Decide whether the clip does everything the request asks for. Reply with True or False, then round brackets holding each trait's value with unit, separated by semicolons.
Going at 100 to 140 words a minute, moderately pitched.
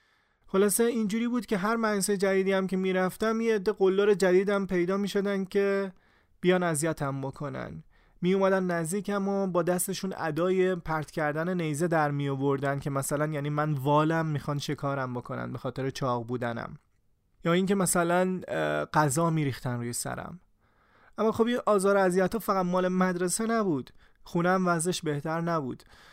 False (155 wpm; 180 Hz)